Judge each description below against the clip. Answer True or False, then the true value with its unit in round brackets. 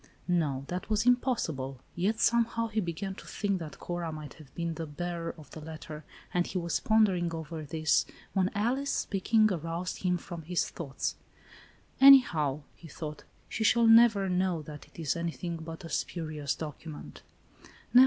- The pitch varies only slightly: False (4.2 semitones)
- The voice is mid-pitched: True (170 Hz)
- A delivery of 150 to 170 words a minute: True (165 wpm)